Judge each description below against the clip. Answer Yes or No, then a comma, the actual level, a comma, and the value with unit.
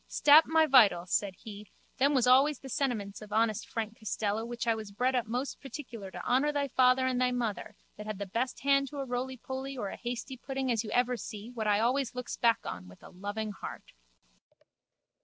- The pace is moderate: No, fast, 215 wpm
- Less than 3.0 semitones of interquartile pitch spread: No, average, 3.7 semitones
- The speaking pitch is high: Yes, high, 245 Hz